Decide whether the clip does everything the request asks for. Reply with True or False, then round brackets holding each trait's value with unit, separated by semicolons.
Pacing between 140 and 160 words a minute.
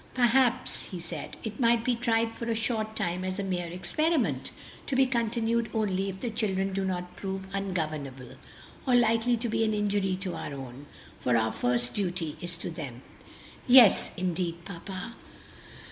False (170 wpm)